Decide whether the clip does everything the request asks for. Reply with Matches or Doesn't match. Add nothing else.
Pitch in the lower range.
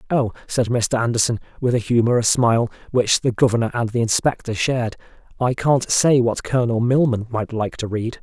Matches